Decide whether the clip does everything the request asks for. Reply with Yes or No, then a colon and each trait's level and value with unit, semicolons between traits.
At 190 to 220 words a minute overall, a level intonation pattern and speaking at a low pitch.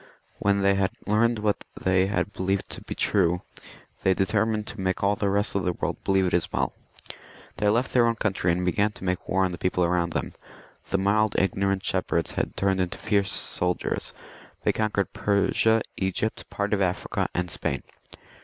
No: average, 180 wpm; narrow, 2.1 semitones; low, 100 Hz